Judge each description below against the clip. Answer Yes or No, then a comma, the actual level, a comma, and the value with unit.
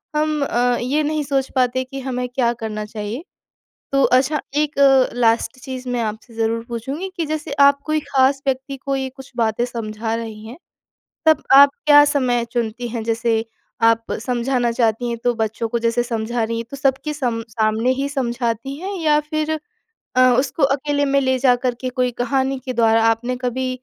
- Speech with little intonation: No, average, 3.1 semitones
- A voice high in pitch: Yes, very high, 250 Hz